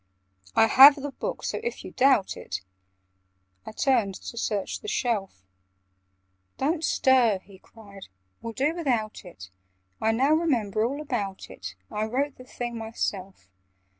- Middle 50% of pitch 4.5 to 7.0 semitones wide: Yes, wide, 5.4 semitones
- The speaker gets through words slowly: No, average, 145 wpm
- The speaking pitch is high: Yes, high, 230 Hz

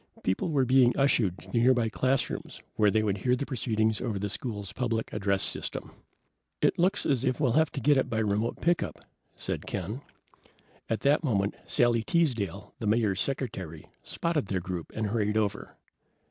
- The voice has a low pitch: Yes, low, 115 Hz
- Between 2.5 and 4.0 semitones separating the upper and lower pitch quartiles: No, average, 4.4 semitones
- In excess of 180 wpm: No, average, 175 wpm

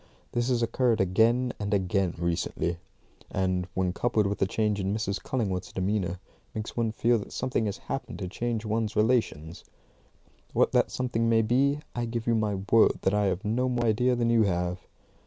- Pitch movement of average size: Yes, average, 3.7 semitones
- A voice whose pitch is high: No, low, 110 Hz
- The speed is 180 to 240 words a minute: Yes, average, 185 wpm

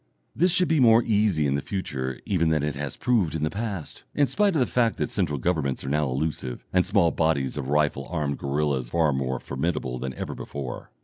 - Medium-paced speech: No, fast, 215 wpm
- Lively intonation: Yes, wide, 6.5 semitones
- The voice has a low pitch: Yes, very low, 75 Hz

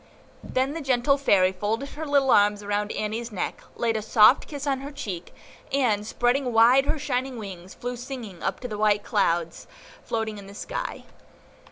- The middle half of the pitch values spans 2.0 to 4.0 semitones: No, average, 4.6 semitones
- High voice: Yes, high, 230 Hz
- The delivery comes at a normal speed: Yes, average, 180 wpm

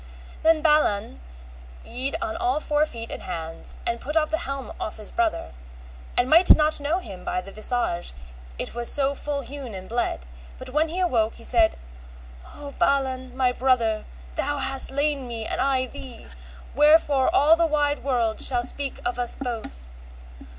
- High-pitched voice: Yes, very high, 265 Hz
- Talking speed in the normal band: Yes, average, 170 wpm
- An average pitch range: Yes, average, 4.1 semitones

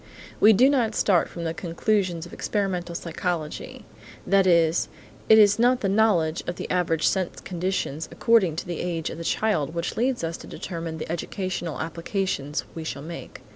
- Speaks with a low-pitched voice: No, medium, 175 Hz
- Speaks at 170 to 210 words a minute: Yes, average, 175 wpm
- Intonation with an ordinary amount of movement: Yes, average, 3.4 semitones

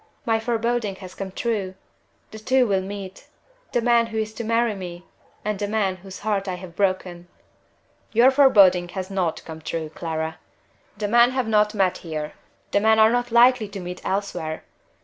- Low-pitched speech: No, high, 200 Hz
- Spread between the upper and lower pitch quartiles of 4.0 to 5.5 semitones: No, average, 3.6 semitones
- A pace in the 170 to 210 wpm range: Yes, average, 180 wpm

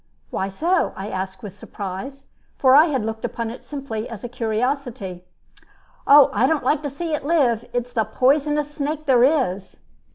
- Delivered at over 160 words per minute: Yes, average, 175 wpm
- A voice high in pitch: Yes, very high, 255 Hz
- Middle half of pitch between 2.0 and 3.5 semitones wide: No, average, 4.8 semitones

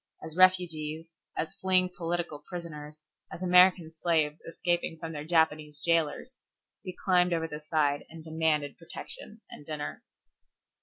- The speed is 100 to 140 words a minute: Yes, slow, 135 wpm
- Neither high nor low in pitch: Yes, medium, 165 Hz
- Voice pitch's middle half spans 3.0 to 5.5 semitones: No, narrow, 2.5 semitones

